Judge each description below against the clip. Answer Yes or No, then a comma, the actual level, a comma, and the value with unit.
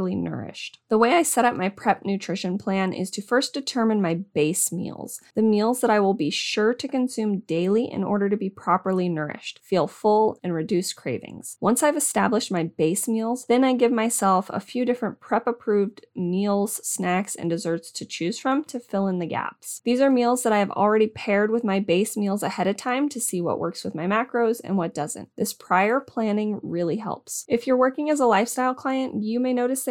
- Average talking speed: No, fast, 215 wpm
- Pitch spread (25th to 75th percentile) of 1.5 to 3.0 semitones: No, average, 4.5 semitones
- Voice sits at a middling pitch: No, high, 210 Hz